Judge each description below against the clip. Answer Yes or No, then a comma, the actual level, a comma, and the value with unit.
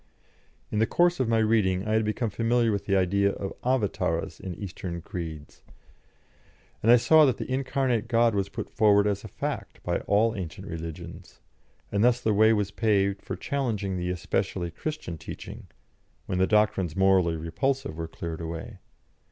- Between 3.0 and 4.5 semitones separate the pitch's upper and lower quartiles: Yes, average, 4.0 semitones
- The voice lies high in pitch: No, low, 100 Hz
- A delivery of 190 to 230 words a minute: No, average, 170 wpm